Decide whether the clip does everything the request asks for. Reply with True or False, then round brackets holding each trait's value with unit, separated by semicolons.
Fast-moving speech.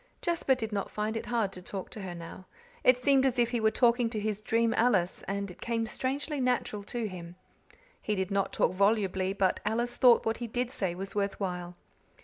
True (215 wpm)